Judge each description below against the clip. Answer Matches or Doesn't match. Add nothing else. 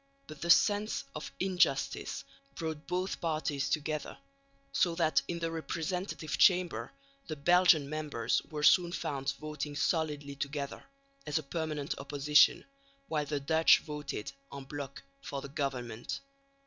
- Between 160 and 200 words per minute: Doesn't match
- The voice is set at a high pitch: Doesn't match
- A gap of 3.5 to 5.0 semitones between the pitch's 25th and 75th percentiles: Doesn't match